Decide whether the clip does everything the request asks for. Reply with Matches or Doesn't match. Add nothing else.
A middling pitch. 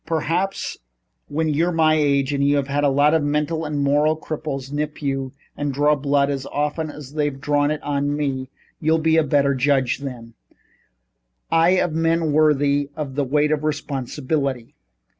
Matches